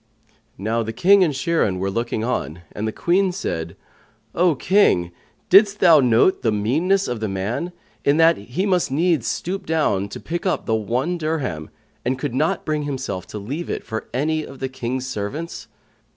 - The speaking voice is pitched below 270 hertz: Yes, low, 135 Hz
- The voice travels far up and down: Yes, wide, 7.3 semitones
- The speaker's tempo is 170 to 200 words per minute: Yes, average, 180 wpm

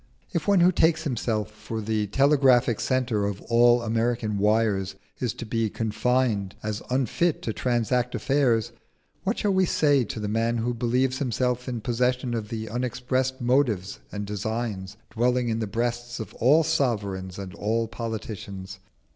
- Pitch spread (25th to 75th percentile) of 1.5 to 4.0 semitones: Yes, average, 3.0 semitones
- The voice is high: No, low, 115 Hz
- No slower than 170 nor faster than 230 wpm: No, average, 155 wpm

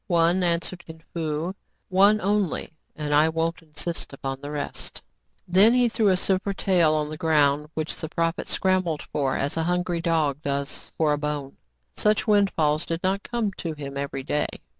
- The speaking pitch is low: No, medium, 165 Hz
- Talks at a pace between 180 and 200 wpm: Yes, average, 185 wpm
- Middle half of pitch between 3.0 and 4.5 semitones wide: Yes, average, 3.7 semitones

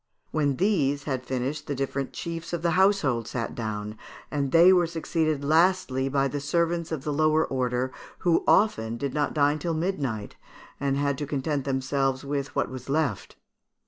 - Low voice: No, medium, 145 Hz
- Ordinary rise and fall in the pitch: Yes, average, 3.5 semitones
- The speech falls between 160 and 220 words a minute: Yes, average, 170 wpm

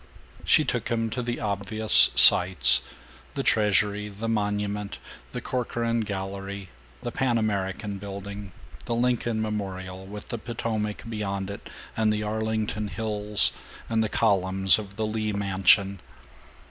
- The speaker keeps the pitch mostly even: Yes, narrow, 1.9 semitones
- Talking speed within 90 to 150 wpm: Yes, slow, 135 wpm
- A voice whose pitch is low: Yes, low, 105 Hz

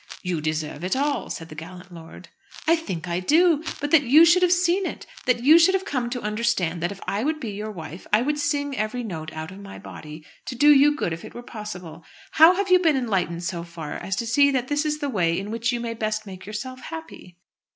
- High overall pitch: Yes, high, 230 Hz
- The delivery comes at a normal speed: No, fast, 245 wpm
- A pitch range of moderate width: No, wide, 8.5 semitones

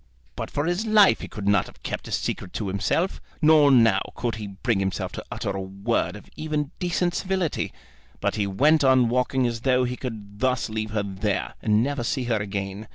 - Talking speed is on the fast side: Yes, fast, 210 wpm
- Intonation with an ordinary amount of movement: No, wide, 5.9 semitones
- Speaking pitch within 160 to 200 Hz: No, low, 120 Hz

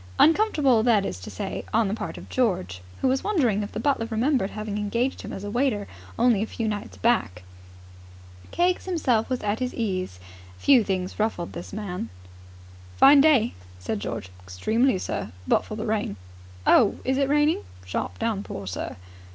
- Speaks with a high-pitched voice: Yes, high, 220 Hz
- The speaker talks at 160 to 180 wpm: Yes, average, 175 wpm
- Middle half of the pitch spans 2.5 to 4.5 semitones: No, average, 5.1 semitones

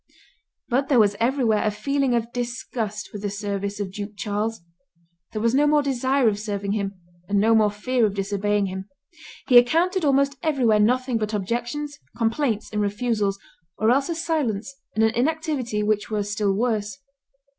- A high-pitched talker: Yes, high, 225 Hz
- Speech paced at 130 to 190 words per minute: Yes, average, 170 wpm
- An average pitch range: Yes, average, 4.0 semitones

